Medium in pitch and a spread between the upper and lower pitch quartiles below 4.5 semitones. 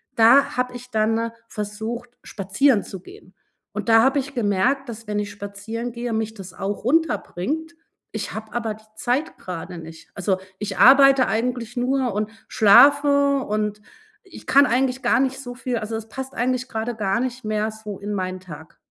No: high, 225 Hz; average, 3.7 semitones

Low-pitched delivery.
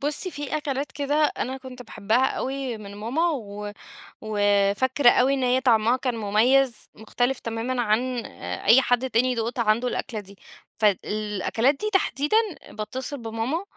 No: high, 245 Hz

